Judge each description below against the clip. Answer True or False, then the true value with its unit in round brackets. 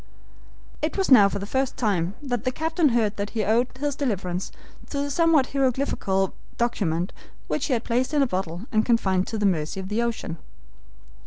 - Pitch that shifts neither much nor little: False (5.7 semitones)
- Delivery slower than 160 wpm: False (190 wpm)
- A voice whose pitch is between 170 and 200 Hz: False (230 Hz)